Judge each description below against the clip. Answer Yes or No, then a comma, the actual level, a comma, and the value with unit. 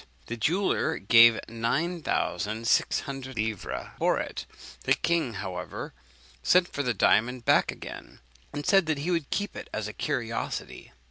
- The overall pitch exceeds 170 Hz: No, low, 125 Hz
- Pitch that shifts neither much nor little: No, wide, 6.3 semitones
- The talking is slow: No, average, 150 wpm